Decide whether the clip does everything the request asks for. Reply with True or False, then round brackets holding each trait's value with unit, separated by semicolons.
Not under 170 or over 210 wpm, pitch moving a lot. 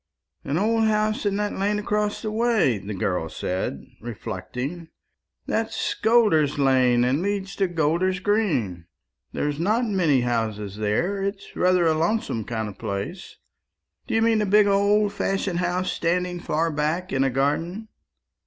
False (155 wpm; 7.6 semitones)